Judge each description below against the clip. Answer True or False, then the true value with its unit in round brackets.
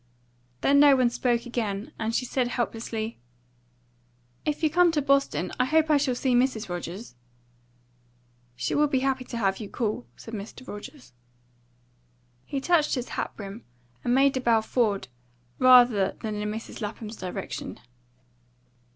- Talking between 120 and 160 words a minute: True (150 wpm)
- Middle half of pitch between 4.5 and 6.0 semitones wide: False (3.9 semitones)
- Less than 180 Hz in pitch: False (240 Hz)